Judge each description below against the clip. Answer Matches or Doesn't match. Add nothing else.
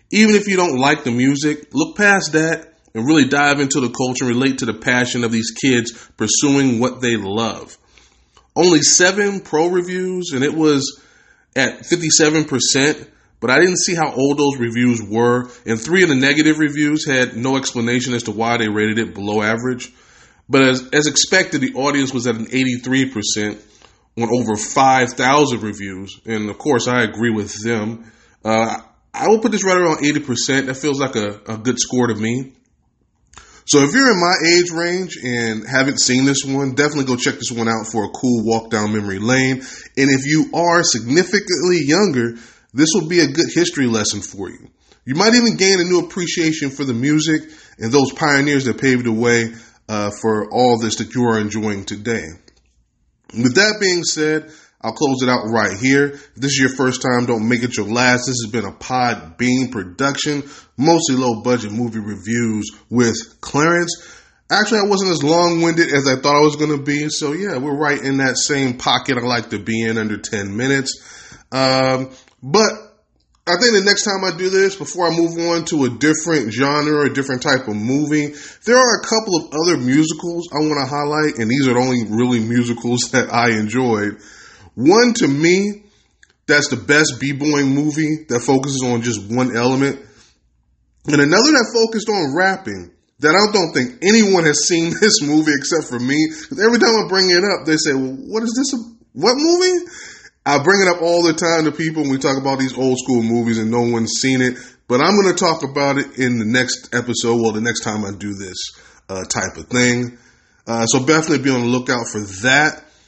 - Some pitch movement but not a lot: Matches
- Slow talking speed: Doesn't match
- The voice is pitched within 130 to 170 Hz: Matches